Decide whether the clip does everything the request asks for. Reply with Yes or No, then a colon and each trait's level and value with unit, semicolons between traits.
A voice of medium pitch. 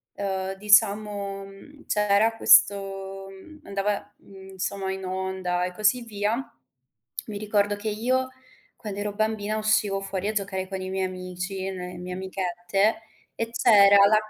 No: high, 200 Hz